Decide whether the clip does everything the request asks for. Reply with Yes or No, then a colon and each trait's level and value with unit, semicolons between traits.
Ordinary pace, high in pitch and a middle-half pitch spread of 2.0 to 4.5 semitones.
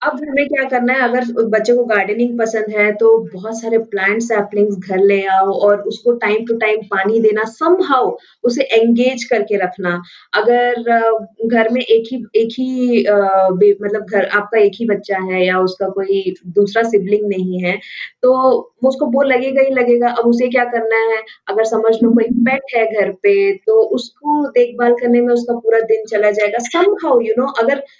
Yes: average, 180 wpm; high, 225 Hz; average, 3.0 semitones